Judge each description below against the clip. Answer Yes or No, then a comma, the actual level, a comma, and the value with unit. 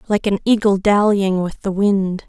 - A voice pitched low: No, high, 200 Hz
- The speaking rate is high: No, average, 185 wpm